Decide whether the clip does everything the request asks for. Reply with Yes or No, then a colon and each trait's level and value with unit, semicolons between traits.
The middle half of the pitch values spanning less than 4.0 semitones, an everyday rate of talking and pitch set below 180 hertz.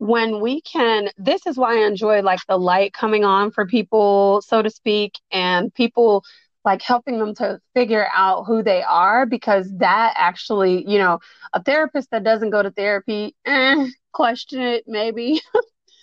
No: average, 3.5 semitones; average, 170 wpm; high, 220 Hz